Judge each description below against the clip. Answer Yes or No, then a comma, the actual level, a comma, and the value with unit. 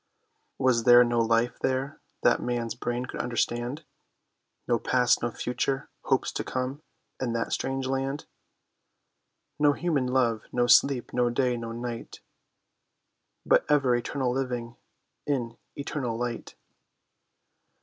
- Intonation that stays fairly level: Yes, narrow, 2.0 semitones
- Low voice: Yes, low, 125 Hz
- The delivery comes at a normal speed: No, slow, 125 wpm